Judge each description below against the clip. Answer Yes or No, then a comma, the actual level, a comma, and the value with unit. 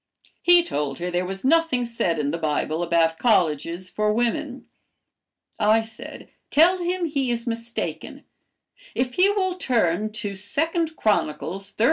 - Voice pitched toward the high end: Yes, high, 220 Hz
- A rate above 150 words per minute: No, average, 145 wpm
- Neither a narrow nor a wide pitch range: No, wide, 8.9 semitones